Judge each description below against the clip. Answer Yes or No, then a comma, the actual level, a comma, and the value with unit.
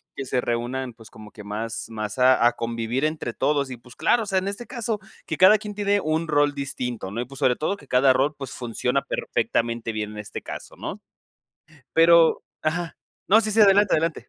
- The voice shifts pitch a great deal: Yes, wide, 6.2 semitones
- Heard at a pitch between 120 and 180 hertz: Yes, low, 135 Hz